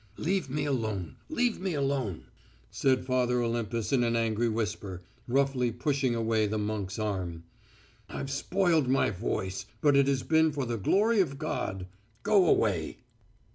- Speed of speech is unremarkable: Yes, average, 150 wpm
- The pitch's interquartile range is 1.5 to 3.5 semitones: No, average, 4.7 semitones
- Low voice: Yes, low, 125 Hz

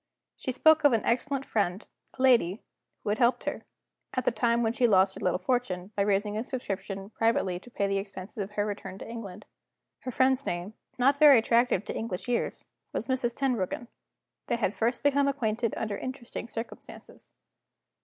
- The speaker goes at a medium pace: Yes, average, 185 wpm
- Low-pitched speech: No, high, 230 Hz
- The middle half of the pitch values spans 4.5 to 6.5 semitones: No, average, 4.1 semitones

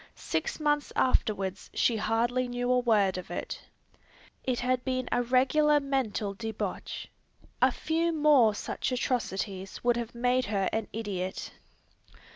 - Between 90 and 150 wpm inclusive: Yes, slow, 135 wpm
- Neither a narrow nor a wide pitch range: Yes, average, 3.5 semitones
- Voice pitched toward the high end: Yes, high, 245 Hz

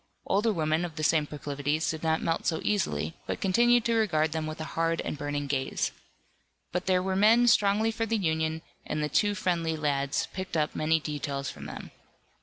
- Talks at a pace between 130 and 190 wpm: No, average, 200 wpm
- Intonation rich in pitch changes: No, average, 4.2 semitones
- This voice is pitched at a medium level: Yes, medium, 160 Hz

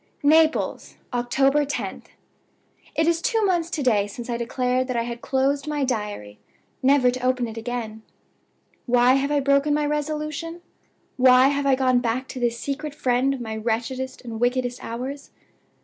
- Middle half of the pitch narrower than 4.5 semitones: Yes, average, 2.9 semitones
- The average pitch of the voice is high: Yes, very high, 255 Hz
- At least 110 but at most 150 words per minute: No, average, 165 wpm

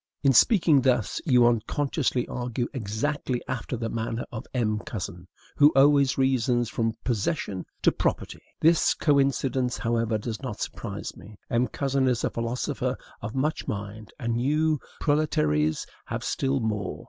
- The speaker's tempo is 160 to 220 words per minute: No, average, 145 wpm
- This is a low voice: Yes, low, 125 Hz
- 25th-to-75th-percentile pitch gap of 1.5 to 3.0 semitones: No, average, 3.7 semitones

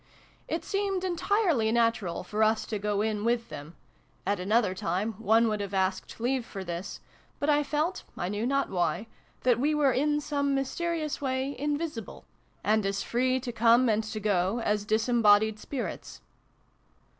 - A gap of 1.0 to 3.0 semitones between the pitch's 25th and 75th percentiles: No, average, 5.2 semitones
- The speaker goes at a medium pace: Yes, average, 165 wpm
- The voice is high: Yes, high, 230 Hz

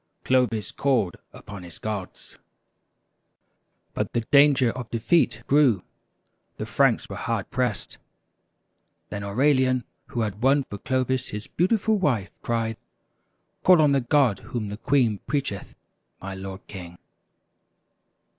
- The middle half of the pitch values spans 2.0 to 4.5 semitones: No, average, 5.1 semitones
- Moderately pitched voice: No, low, 120 Hz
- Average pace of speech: No, slow, 125 wpm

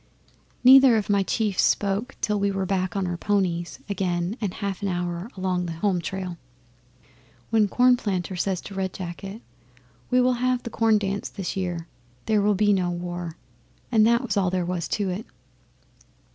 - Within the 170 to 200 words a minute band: Yes, average, 175 wpm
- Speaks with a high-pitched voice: Yes, high, 195 Hz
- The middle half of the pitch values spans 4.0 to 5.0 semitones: No, average, 2.9 semitones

